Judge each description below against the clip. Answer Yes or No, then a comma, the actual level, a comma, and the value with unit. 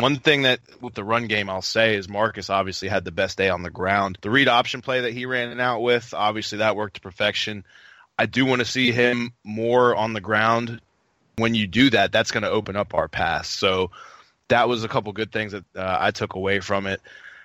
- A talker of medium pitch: No, low, 110 Hz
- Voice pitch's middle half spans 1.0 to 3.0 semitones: No, average, 3.4 semitones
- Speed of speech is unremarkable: No, fast, 235 wpm